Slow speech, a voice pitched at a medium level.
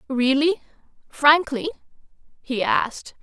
No: slow, 75 wpm; very high, 280 Hz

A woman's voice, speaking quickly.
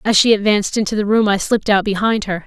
Yes: female; fast, 270 wpm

